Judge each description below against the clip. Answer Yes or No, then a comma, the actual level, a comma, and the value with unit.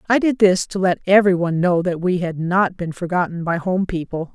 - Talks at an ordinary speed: No, fast, 220 wpm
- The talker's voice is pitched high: No, medium, 180 Hz